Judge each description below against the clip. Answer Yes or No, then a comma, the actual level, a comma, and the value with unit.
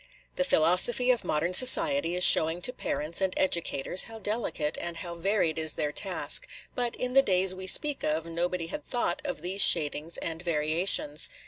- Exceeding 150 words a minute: Yes, average, 180 wpm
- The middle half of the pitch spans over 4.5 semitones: Yes, wide, 5.4 semitones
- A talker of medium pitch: Yes, medium, 180 Hz